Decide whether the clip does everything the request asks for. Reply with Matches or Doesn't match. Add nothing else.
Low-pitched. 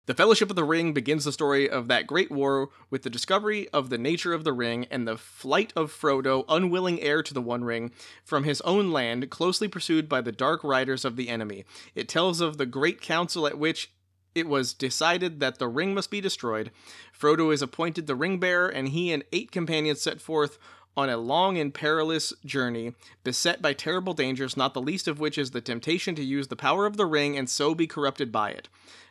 Doesn't match